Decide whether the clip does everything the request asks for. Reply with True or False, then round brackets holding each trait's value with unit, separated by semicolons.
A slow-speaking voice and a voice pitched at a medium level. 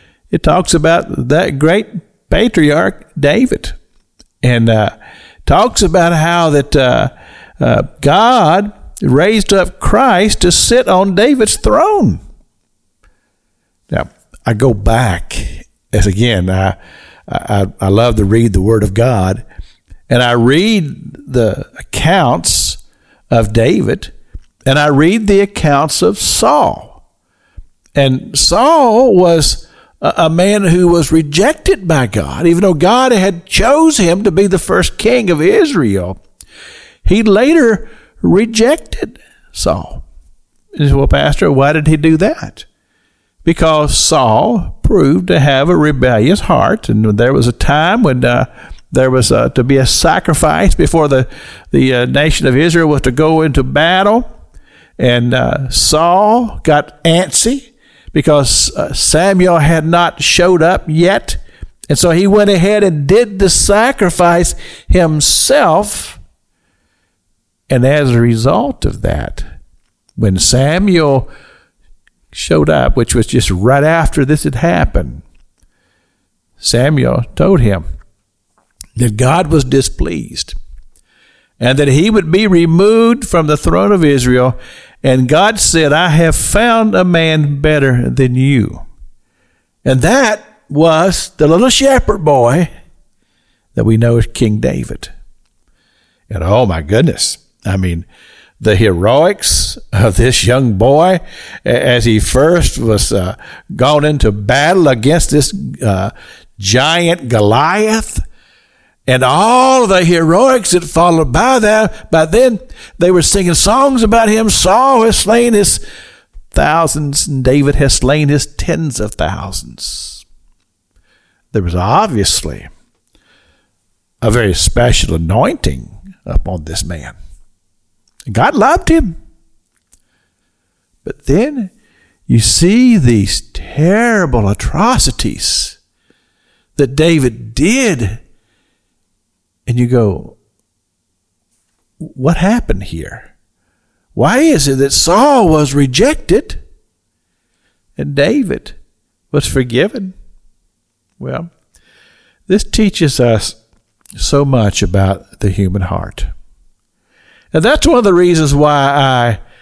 True (120 wpm; 145 Hz)